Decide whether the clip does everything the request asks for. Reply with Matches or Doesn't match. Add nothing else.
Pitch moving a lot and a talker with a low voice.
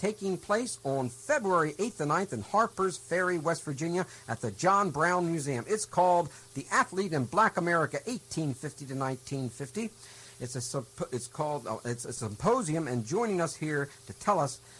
Doesn't match